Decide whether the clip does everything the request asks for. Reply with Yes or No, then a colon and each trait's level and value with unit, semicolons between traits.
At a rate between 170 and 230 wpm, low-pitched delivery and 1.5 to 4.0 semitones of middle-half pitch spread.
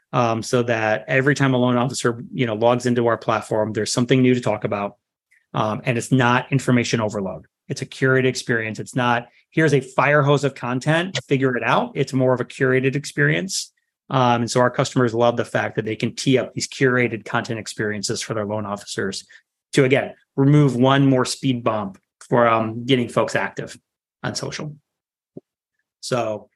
Yes: average, 190 wpm; low, 125 Hz; average, 2.9 semitones